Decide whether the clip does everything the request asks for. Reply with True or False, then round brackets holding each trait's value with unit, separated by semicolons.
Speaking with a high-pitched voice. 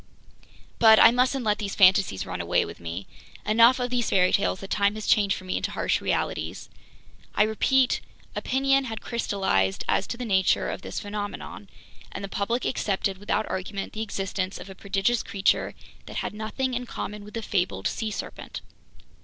True (210 Hz)